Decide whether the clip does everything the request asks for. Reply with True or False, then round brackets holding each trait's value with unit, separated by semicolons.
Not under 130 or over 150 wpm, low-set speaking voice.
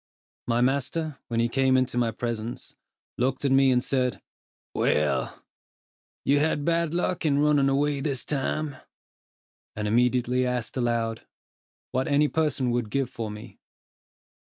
True (140 wpm; 130 Hz)